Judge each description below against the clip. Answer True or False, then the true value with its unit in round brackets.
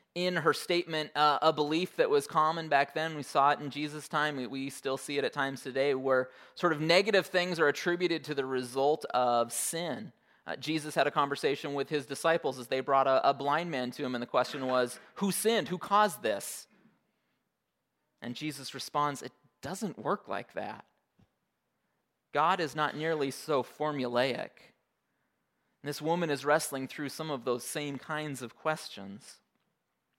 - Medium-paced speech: True (180 wpm)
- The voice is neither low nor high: True (145 Hz)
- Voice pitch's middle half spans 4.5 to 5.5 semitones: False (3.2 semitones)